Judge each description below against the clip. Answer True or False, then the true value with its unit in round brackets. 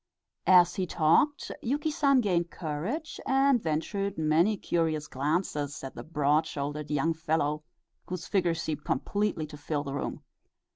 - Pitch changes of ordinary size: True (4.9 semitones)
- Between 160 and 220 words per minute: False (145 wpm)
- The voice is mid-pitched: True (165 Hz)